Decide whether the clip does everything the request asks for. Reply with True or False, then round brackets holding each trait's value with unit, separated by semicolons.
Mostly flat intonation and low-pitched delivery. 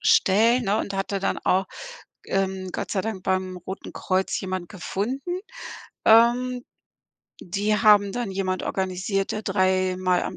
False (2.3 semitones; 195 Hz)